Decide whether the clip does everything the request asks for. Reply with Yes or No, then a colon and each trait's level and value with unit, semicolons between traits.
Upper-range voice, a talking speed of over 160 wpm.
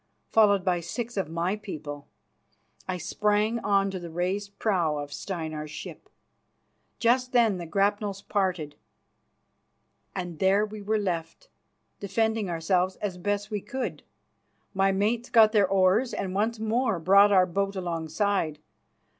No: high, 195 Hz; average, 140 wpm